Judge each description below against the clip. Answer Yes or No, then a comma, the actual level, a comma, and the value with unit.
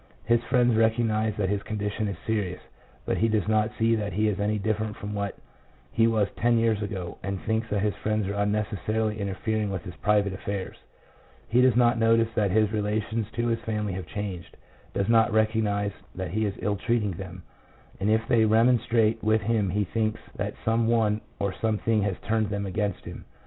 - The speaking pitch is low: Yes, low, 110 Hz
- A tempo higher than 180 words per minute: Yes, average, 195 wpm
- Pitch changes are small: Yes, narrow, 1.7 semitones